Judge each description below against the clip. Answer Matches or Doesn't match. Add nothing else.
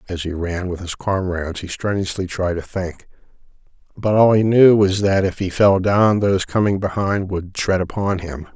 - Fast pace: Doesn't match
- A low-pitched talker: Matches